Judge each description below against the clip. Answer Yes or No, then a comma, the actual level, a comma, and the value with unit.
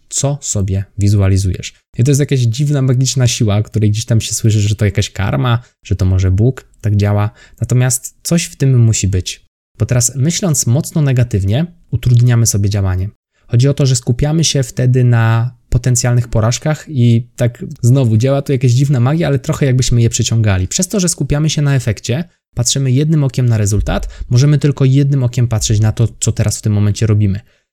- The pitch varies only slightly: No, average, 4.3 semitones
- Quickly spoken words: Yes, fast, 190 wpm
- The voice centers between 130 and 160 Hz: No, low, 120 Hz